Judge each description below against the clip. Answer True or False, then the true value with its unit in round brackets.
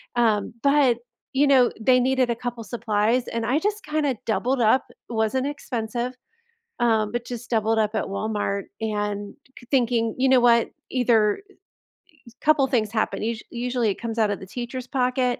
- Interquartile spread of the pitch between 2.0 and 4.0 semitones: True (2.6 semitones)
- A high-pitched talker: True (240 Hz)